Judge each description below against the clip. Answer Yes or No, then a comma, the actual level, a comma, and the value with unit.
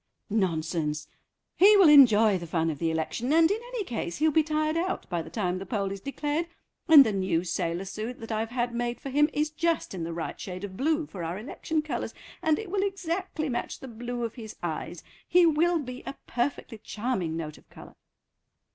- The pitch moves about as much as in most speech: No, wide, 8.6 semitones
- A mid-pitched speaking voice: No, high, 240 Hz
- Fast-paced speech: Yes, fast, 210 wpm